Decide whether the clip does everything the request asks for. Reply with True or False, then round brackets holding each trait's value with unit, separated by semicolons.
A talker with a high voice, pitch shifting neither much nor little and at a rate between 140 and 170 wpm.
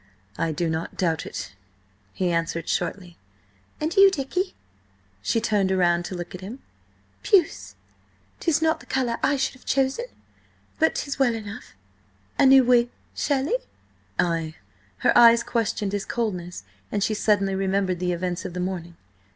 False (205 Hz; 6.9 semitones; 155 wpm)